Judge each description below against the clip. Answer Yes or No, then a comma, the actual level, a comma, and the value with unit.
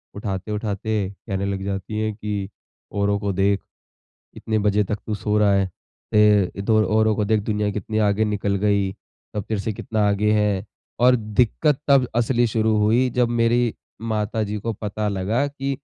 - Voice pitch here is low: Yes, low, 105 Hz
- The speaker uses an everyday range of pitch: No, narrow, 1.7 semitones